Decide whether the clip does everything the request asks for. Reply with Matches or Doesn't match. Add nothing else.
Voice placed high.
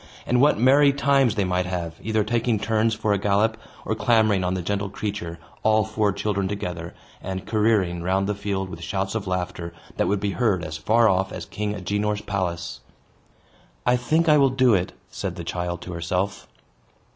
Doesn't match